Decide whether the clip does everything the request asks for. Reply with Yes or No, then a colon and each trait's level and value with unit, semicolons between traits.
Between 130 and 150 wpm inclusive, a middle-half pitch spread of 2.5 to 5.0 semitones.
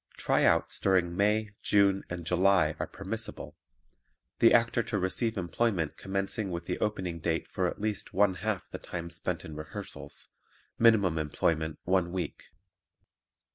Yes: average, 140 wpm; average, 3.4 semitones